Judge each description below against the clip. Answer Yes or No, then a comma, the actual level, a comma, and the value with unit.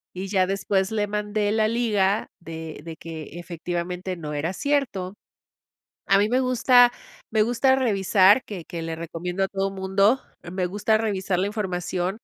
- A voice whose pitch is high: Yes, high, 195 Hz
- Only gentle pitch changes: No, average, 3.3 semitones